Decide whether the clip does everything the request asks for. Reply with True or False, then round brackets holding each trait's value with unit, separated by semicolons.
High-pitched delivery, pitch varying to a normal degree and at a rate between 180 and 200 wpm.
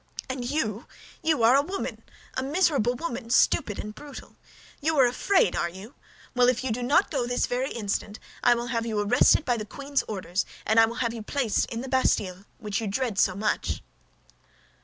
True (240 Hz; 3.8 semitones; 195 wpm)